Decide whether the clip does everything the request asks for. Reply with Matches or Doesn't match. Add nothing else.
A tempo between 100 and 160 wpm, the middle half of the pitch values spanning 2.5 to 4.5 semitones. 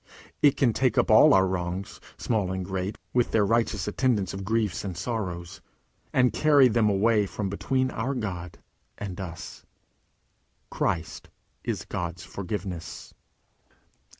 Matches